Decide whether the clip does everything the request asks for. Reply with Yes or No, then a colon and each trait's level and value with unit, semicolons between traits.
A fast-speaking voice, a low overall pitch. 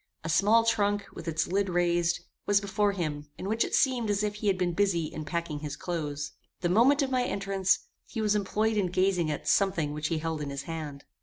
No: fast, 225 wpm; medium, 185 Hz